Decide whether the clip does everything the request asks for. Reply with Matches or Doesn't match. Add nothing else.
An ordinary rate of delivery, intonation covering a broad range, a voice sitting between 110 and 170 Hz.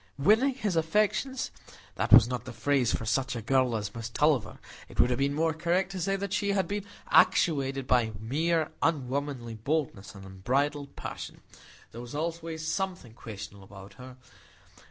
Matches